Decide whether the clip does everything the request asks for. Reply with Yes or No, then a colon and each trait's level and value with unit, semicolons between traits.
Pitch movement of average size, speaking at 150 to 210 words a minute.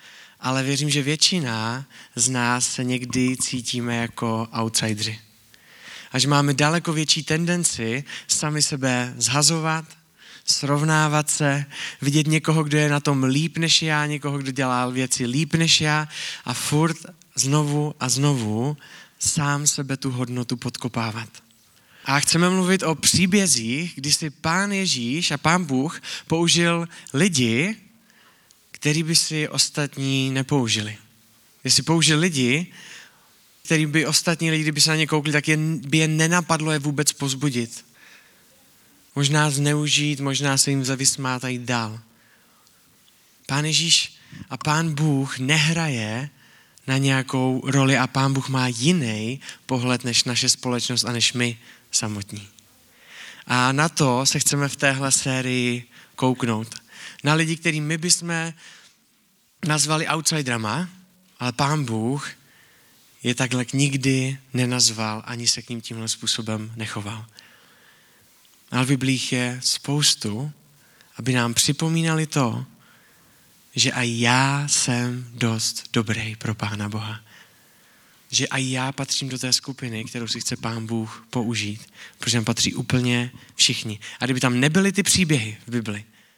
No: average, 4.0 semitones; average, 130 wpm